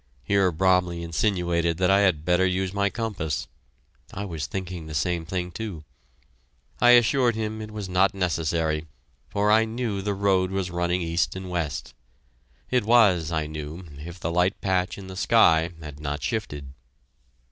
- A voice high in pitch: No, very low, 90 Hz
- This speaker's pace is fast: No, average, 165 wpm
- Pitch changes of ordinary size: Yes, average, 3.4 semitones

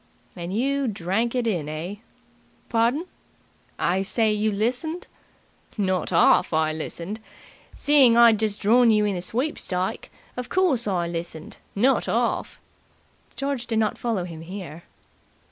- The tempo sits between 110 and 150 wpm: Yes, slow, 135 wpm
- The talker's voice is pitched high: Yes, high, 210 Hz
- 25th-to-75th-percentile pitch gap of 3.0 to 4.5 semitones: No, average, 5.2 semitones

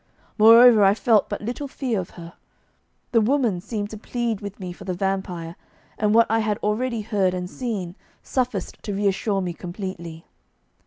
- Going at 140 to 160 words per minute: No, average, 170 wpm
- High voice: Yes, high, 205 Hz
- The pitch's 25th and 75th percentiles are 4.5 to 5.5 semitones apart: No, average, 3.5 semitones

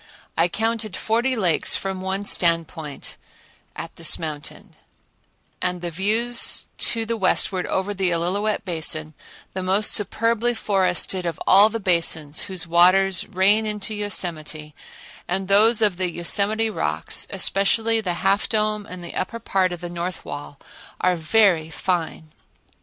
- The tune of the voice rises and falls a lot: No, average, 3.6 semitones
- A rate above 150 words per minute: No, average, 140 wpm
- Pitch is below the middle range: No, high, 190 Hz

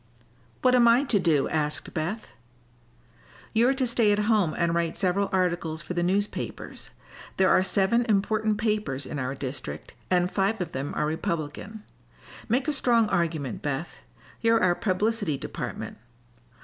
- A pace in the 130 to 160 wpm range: Yes, average, 150 wpm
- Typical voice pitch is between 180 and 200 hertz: Yes, high, 190 Hz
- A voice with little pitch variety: No, wide, 5.5 semitones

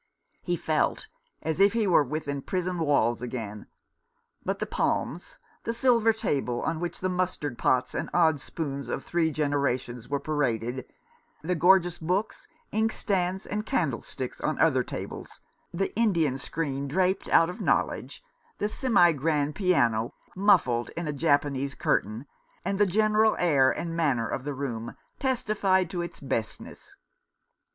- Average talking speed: Yes, average, 145 wpm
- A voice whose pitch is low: No, medium, 160 Hz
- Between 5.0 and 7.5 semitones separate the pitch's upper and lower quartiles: Yes, wide, 5.6 semitones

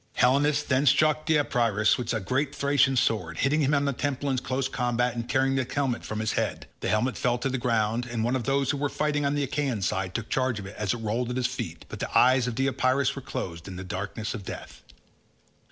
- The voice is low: Yes, low, 125 Hz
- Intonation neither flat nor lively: Yes, average, 3.6 semitones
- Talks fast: Yes, fast, 240 wpm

